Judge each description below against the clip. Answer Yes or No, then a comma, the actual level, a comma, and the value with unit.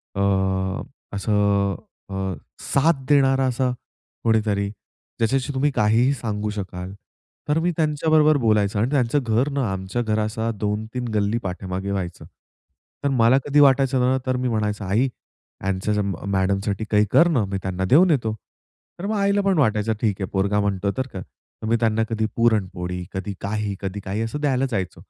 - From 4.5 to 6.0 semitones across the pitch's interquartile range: Yes, average, 4.9 semitones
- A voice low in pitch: Yes, low, 110 Hz